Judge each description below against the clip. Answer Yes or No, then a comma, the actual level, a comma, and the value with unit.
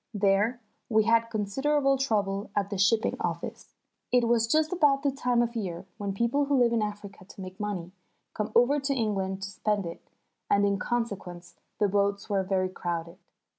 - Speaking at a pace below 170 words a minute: No, average, 180 wpm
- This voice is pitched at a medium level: No, high, 210 Hz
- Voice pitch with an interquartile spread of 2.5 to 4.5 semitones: Yes, average, 3.6 semitones